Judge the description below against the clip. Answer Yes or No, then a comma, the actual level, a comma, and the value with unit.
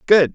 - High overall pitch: No, medium, 170 Hz